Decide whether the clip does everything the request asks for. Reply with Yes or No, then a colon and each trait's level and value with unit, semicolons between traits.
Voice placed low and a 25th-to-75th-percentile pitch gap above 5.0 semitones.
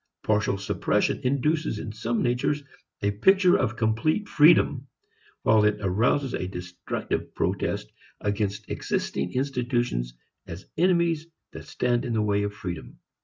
Yes: low, 115 Hz; wide, 5.6 semitones